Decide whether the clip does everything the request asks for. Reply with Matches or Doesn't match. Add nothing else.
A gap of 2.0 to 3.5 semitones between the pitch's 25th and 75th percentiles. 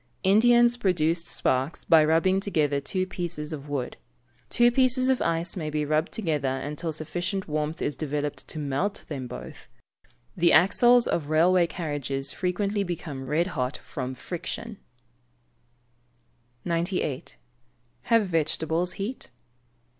Doesn't match